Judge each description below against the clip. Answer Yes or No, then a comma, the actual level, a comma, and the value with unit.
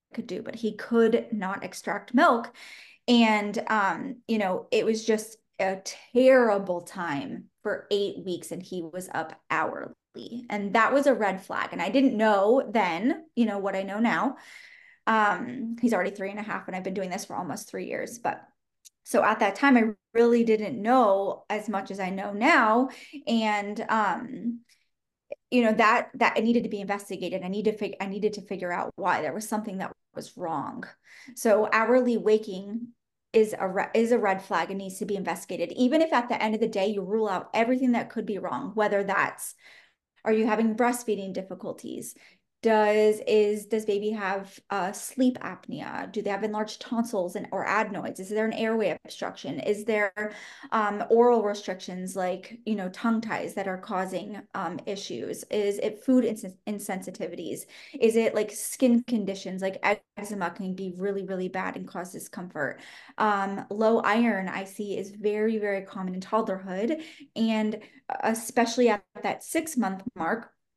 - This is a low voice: No, high, 215 Hz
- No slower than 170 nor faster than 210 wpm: Yes, average, 180 wpm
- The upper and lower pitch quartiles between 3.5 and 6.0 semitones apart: No, average, 3.0 semitones